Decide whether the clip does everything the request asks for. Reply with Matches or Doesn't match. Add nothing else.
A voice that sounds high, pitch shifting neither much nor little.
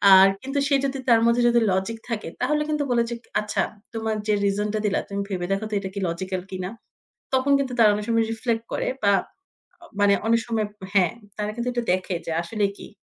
Matches